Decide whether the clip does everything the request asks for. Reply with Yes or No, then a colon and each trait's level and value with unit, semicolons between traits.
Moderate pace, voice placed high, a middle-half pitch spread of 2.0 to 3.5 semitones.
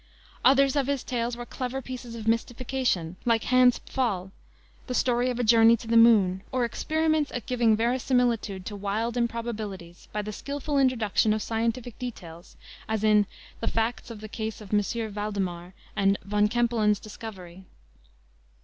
Yes: average, 160 wpm; high, 230 Hz; average, 3.0 semitones